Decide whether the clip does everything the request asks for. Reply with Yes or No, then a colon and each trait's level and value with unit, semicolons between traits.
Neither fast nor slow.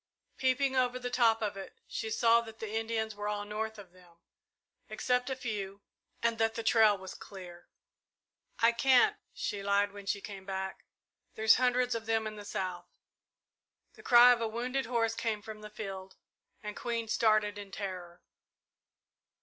Yes: average, 170 wpm